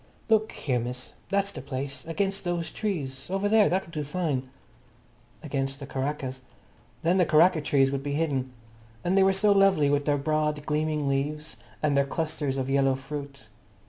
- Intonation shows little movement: No, average, 4.3 semitones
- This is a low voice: No, medium, 150 Hz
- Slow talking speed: No, average, 175 wpm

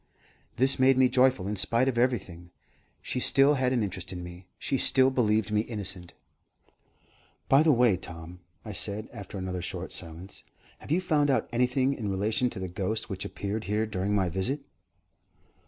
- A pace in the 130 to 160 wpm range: No, average, 175 wpm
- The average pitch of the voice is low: Yes, low, 110 Hz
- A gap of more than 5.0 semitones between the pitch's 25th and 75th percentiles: Yes, wide, 5.5 semitones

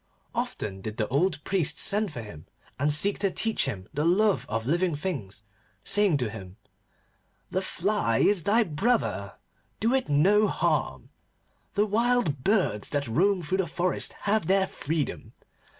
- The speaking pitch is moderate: Yes, medium, 170 Hz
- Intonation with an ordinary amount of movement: No, wide, 7.3 semitones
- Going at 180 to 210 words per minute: No, average, 155 wpm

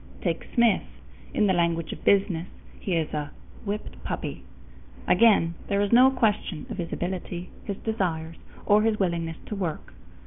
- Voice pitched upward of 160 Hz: Yes, high, 190 Hz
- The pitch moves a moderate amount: Yes, average, 4.0 semitones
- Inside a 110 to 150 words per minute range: No, average, 160 wpm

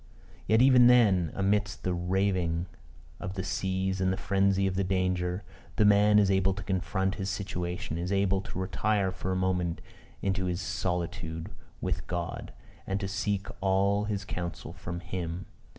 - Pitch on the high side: No, very low, 95 Hz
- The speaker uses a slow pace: No, average, 160 wpm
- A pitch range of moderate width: No, narrow, 1.7 semitones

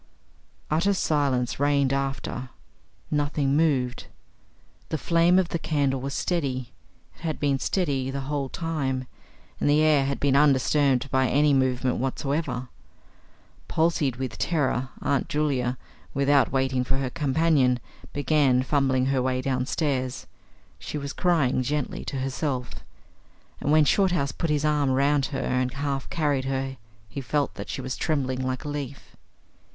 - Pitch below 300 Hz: Yes, medium, 140 Hz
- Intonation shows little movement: Yes, narrow, 2.3 semitones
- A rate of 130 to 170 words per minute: Yes, average, 145 wpm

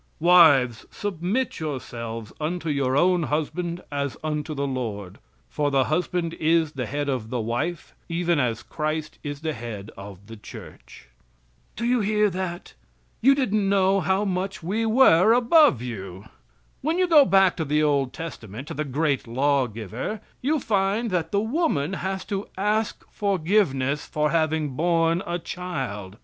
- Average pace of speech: Yes, average, 160 wpm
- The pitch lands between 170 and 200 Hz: No, medium, 160 Hz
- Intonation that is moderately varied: No, wide, 6.3 semitones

